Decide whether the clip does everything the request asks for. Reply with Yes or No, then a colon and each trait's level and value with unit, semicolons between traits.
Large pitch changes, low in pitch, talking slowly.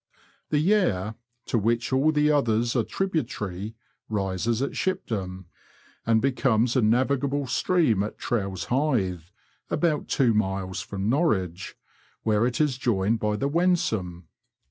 Yes: wide, 6.1 semitones; low, 115 Hz; slow, 130 wpm